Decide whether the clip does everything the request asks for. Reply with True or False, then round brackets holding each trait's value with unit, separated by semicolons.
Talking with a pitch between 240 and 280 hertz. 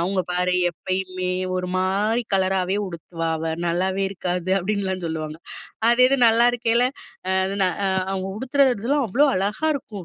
False (190 Hz)